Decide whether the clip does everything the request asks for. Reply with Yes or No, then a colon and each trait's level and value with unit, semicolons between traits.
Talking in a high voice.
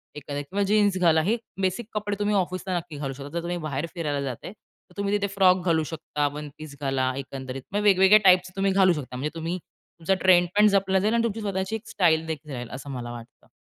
No: medium, 175 Hz